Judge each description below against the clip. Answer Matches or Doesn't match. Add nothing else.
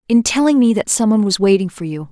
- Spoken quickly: Matches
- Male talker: Doesn't match